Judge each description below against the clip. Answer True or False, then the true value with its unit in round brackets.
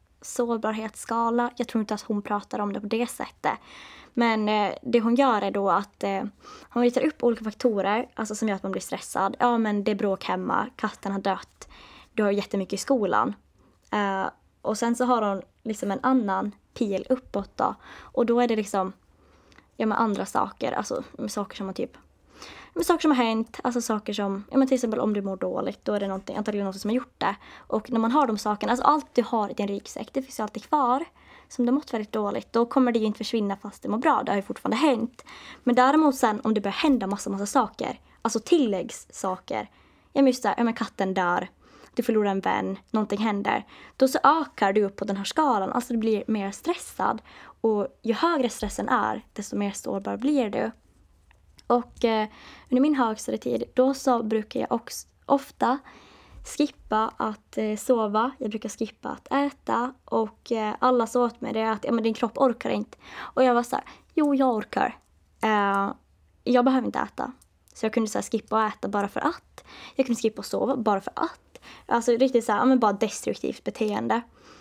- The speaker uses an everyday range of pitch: True (3.4 semitones)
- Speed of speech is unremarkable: False (210 wpm)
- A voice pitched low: False (225 Hz)